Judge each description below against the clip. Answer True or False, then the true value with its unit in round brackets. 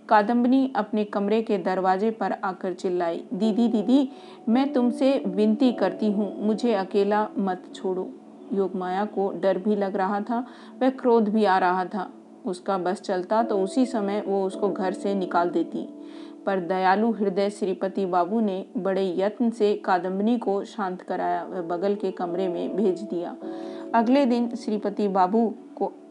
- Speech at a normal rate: True (160 wpm)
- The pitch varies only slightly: False (3.3 semitones)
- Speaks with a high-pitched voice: True (205 Hz)